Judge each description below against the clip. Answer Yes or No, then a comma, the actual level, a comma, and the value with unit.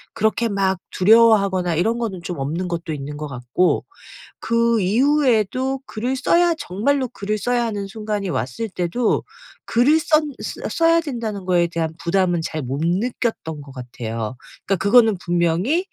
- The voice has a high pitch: Yes, high, 200 Hz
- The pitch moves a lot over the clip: Yes, wide, 5.8 semitones